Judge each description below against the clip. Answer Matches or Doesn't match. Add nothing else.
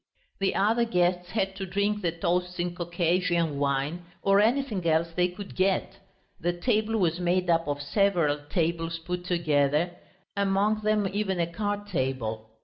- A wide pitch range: Doesn't match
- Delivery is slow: Doesn't match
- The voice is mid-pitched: Matches